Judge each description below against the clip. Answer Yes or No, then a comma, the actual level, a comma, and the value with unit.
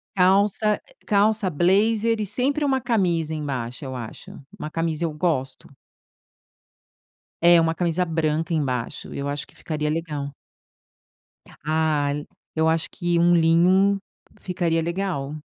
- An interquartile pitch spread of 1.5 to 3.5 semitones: No, average, 4.0 semitones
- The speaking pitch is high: No, medium, 165 Hz